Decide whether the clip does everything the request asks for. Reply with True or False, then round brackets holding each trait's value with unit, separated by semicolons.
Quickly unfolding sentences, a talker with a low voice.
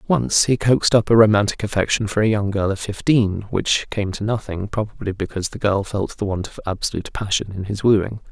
True (215 wpm; 105 Hz)